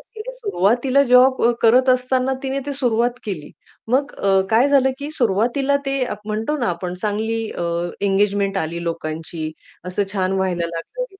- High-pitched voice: Yes, high, 225 Hz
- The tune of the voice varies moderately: No, wide, 5.7 semitones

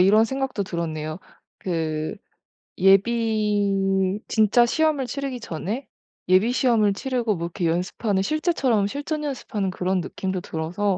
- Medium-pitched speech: No, high, 205 Hz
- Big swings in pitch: No, average, 4.7 semitones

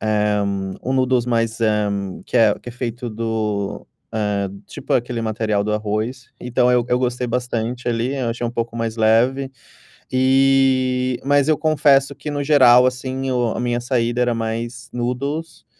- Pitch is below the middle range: Yes, low, 120 Hz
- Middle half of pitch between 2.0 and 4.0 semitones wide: Yes, narrow, 2.4 semitones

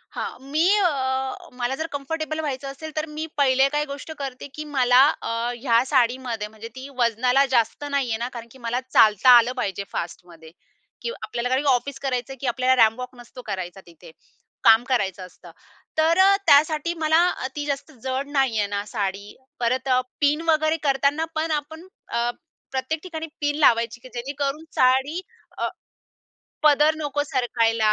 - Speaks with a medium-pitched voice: No, very high, 260 Hz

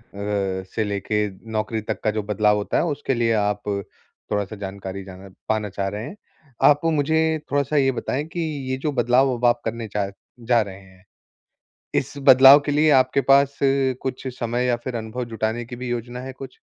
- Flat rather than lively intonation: No, average, 4.2 semitones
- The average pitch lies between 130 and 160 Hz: No, low, 115 Hz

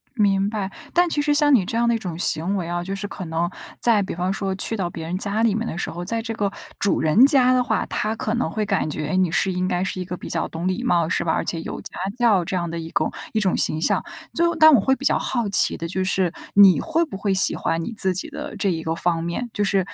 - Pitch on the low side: No, high, 195 Hz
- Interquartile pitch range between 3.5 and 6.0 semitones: Yes, average, 4.6 semitones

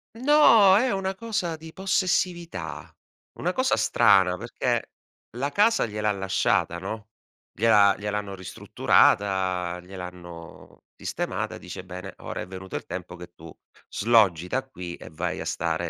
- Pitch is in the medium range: No, low, 100 Hz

